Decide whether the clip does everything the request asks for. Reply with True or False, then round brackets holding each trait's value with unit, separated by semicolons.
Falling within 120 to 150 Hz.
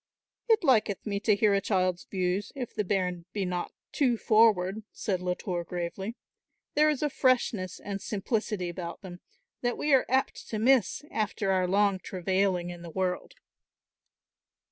False (200 Hz)